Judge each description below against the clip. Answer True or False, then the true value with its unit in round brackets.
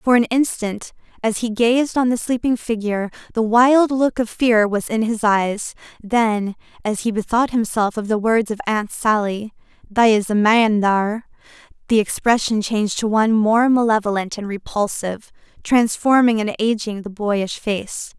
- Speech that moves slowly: False (165 wpm)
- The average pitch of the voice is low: False (220 Hz)